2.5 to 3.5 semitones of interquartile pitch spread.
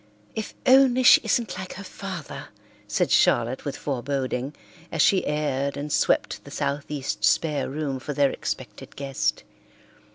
No: average, 5.3 semitones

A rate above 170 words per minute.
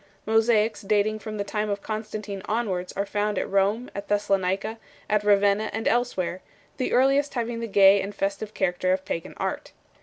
Yes: average, 180 wpm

